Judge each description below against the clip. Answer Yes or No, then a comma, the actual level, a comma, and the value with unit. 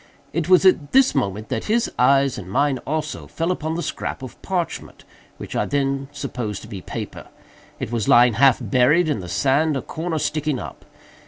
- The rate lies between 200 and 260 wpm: No, average, 190 wpm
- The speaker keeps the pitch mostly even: No, average, 4.5 semitones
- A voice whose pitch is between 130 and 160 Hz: Yes, medium, 140 Hz